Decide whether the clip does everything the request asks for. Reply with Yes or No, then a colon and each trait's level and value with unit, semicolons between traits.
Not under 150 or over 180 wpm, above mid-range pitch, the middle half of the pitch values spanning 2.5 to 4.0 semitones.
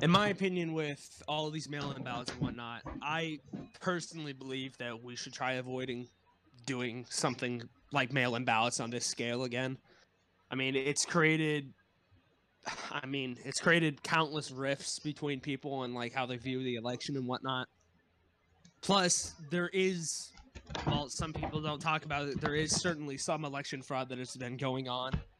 No: average, 170 wpm; low, 135 Hz; average, 3.7 semitones